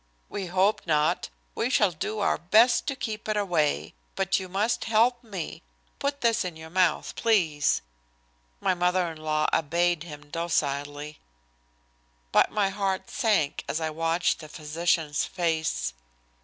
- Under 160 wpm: Yes, average, 145 wpm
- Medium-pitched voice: Yes, medium, 175 Hz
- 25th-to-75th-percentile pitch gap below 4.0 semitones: No, average, 4.8 semitones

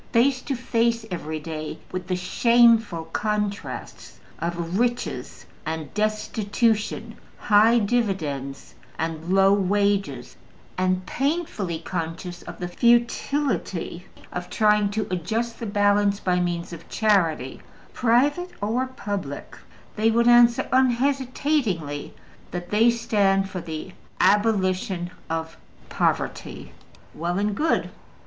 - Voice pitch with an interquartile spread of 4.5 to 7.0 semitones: Yes, average, 4.9 semitones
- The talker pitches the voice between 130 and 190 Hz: No, high, 205 Hz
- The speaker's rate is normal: No, slow, 110 wpm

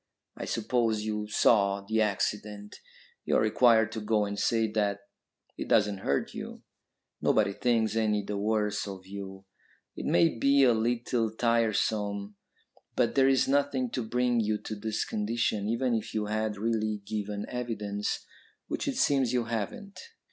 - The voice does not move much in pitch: Yes, narrow, 2.1 semitones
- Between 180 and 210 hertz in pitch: No, low, 110 Hz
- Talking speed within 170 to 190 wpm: No, average, 155 wpm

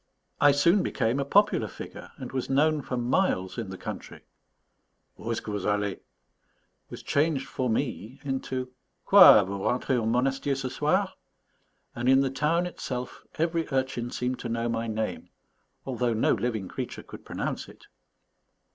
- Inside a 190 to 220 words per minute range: No, average, 160 wpm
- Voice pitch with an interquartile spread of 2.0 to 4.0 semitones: Yes, average, 3.4 semitones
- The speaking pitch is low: Yes, low, 125 Hz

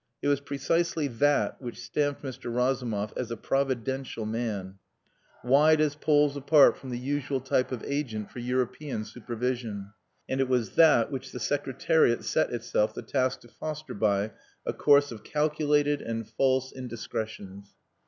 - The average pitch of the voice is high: No, low, 130 Hz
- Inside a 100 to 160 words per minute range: Yes, average, 155 wpm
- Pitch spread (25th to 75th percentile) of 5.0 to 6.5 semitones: No, average, 3.8 semitones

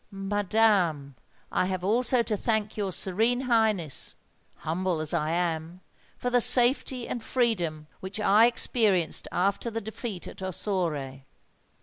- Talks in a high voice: Yes, high, 195 Hz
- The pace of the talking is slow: Yes, slow, 125 wpm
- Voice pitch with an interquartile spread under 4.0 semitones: No, average, 4.6 semitones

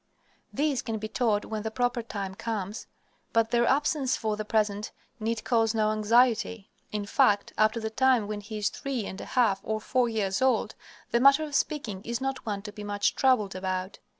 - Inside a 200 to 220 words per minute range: Yes, fast, 205 wpm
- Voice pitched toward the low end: No, high, 220 Hz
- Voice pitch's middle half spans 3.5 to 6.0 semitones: No, average, 3.1 semitones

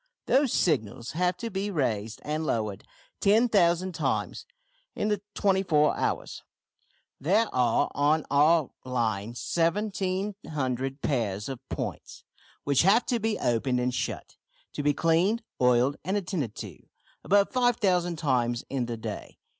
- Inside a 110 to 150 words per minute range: Yes, slow, 135 wpm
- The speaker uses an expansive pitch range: Yes, wide, 7.7 semitones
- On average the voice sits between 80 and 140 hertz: No, medium, 155 Hz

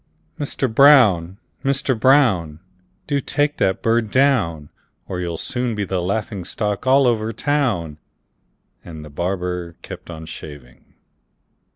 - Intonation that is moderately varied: No, wide, 7.3 semitones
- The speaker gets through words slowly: Yes, slow, 130 wpm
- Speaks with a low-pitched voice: Yes, low, 100 Hz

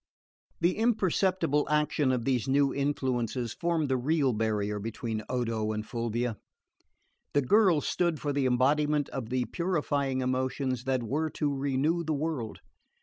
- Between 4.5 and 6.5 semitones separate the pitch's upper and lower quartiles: No, average, 3.7 semitones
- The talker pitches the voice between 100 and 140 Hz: Yes, low, 135 Hz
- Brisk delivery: No, average, 145 wpm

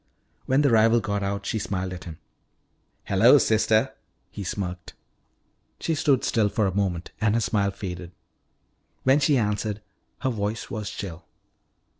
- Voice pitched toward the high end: No, low, 105 Hz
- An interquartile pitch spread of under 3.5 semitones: Yes, average, 2.8 semitones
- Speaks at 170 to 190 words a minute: No, average, 150 wpm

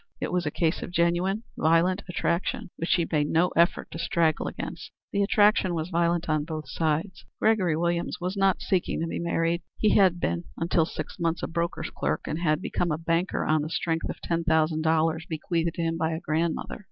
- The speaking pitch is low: No, medium, 170 Hz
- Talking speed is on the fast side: Yes, fast, 210 wpm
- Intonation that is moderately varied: No, narrow, 1.8 semitones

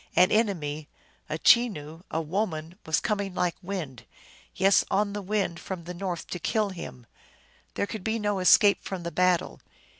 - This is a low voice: No, medium, 185 Hz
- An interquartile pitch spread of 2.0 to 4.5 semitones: Yes, average, 3.7 semitones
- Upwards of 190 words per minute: No, average, 170 wpm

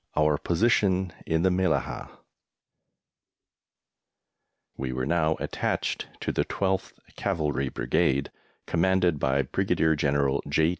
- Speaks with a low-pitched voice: Yes, very low, 80 Hz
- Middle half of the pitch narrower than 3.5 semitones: No, average, 4.6 semitones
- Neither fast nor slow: No, slow, 105 wpm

